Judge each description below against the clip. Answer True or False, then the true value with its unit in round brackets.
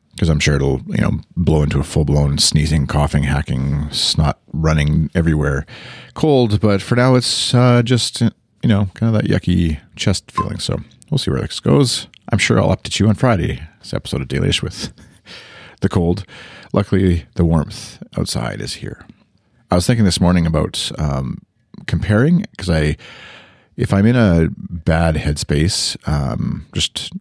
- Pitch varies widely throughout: True (6.0 semitones)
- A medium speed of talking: True (170 wpm)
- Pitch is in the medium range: False (85 Hz)